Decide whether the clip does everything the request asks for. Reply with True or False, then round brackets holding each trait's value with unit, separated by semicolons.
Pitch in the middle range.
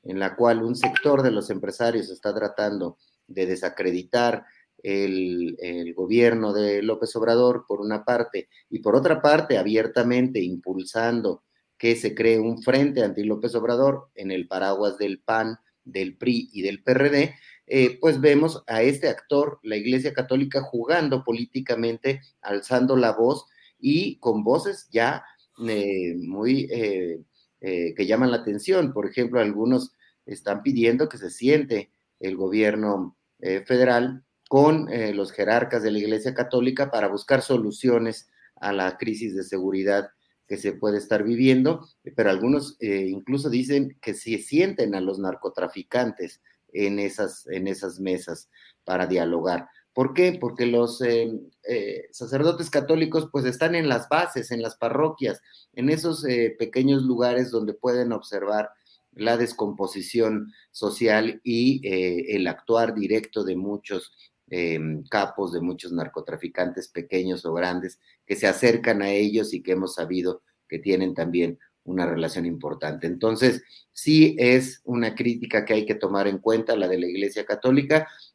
False (115 Hz)